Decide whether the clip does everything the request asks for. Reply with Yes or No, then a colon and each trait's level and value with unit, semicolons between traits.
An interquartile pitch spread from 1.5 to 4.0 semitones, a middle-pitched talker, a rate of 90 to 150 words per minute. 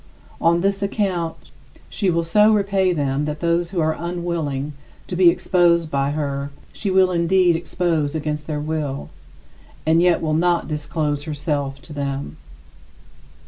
Yes: average, 3.1 semitones; medium, 165 Hz; average, 145 wpm